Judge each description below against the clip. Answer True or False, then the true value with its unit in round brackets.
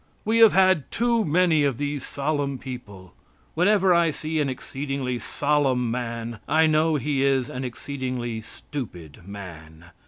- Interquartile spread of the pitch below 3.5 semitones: False (4.6 semitones)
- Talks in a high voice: False (140 Hz)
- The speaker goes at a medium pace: True (145 wpm)